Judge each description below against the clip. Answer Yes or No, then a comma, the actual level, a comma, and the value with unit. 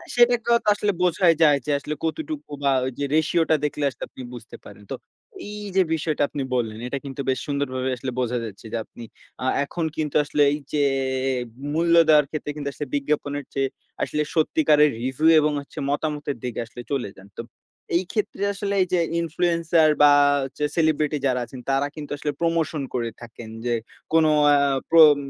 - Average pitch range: Yes, average, 3.2 semitones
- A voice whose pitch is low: No, medium, 150 Hz